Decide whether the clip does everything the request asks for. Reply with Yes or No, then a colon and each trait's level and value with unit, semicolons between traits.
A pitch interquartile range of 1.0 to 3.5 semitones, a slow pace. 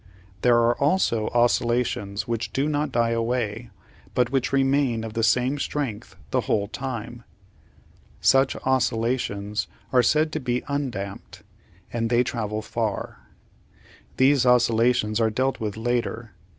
Yes: average, 2.7 semitones; slow, 130 wpm